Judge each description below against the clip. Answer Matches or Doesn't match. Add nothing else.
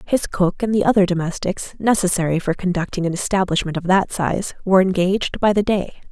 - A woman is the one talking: Matches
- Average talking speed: Matches